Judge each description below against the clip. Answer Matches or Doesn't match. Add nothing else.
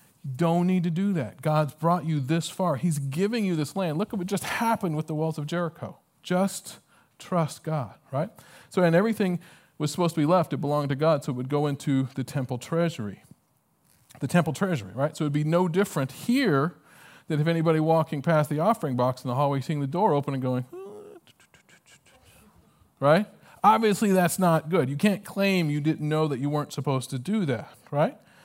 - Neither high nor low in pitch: Matches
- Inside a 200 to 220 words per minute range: Matches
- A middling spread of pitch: Matches